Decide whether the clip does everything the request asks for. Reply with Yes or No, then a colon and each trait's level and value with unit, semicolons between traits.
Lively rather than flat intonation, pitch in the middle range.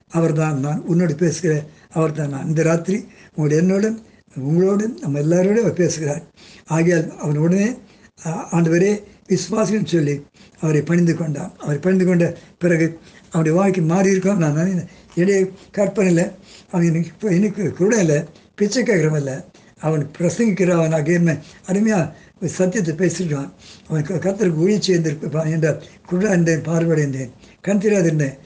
No: average, 3.3 semitones; medium, 170 Hz